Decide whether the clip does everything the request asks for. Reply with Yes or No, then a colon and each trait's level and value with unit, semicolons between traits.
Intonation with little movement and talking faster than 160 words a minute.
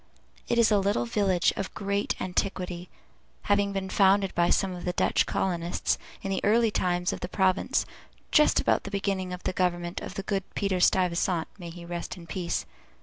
Yes: narrow, 2.0 semitones; average, 190 wpm